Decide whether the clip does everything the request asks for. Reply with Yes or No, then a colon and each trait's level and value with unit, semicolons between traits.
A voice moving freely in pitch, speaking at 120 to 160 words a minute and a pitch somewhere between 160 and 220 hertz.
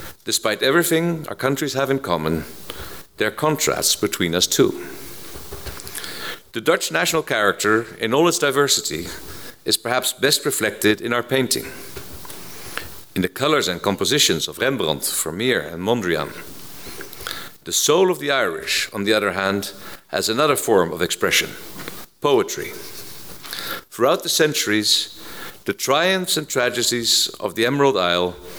No: wide, 7.4 semitones; slow, 135 wpm; low, 125 Hz